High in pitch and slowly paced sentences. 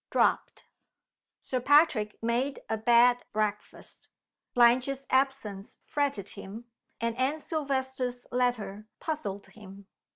Yes: high, 245 Hz; slow, 100 wpm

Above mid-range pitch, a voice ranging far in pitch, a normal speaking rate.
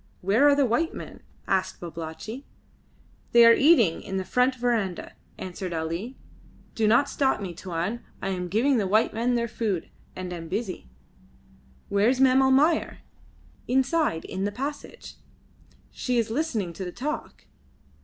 Yes: high, 225 Hz; wide, 5.8 semitones; average, 150 wpm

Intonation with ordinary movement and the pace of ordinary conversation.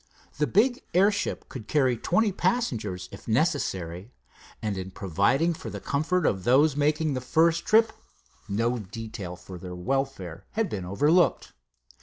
No: wide, 9.0 semitones; average, 145 wpm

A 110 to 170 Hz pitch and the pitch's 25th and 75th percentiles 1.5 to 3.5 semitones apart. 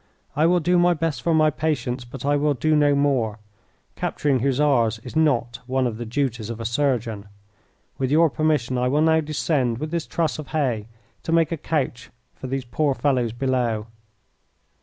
No: low, 135 Hz; average, 4.3 semitones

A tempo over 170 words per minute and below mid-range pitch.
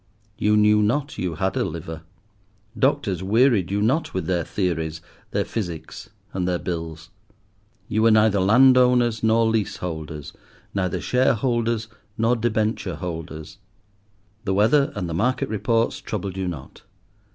No: slow, 135 wpm; low, 105 Hz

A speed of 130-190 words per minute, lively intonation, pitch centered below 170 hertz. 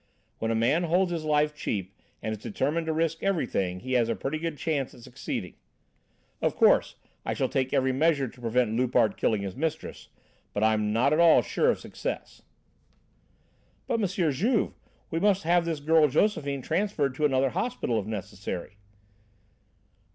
Yes: average, 170 wpm; wide, 6.2 semitones; medium, 140 Hz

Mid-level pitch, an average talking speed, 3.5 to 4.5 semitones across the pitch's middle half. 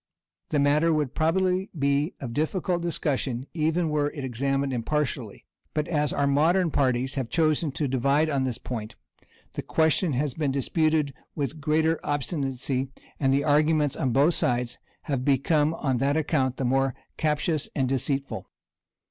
No: medium, 145 Hz; average, 155 wpm; average, 2.7 semitones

